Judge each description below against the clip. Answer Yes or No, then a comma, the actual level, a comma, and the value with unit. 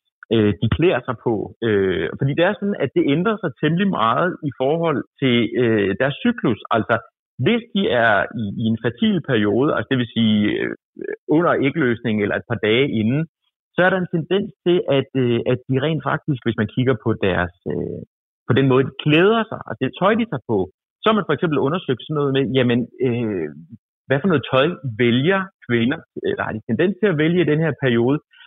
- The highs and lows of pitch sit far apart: Yes, wide, 6.9 semitones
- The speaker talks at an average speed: Yes, average, 215 wpm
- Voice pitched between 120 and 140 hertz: Yes, low, 135 Hz